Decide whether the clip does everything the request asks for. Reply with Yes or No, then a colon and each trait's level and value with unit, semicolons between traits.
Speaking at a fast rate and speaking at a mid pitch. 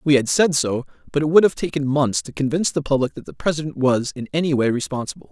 Yes: fast, 250 wpm; medium, 145 Hz